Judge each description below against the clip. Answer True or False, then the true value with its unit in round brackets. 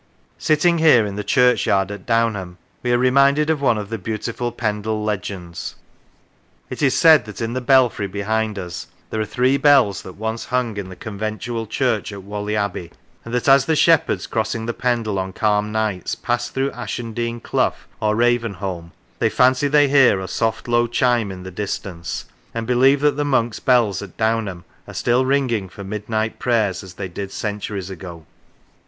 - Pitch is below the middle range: True (110 Hz)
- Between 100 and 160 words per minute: False (185 wpm)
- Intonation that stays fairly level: False (3.6 semitones)